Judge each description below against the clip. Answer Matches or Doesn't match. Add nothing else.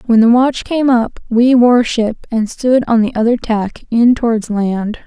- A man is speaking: Doesn't match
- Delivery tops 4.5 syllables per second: Doesn't match